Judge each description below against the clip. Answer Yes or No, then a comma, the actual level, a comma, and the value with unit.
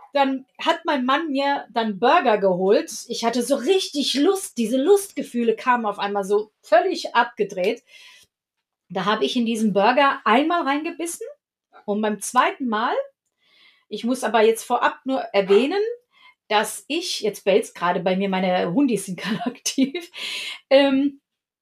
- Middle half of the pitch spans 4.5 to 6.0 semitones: Yes, average, 5.2 semitones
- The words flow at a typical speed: Yes, average, 145 wpm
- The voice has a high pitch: Yes, high, 245 Hz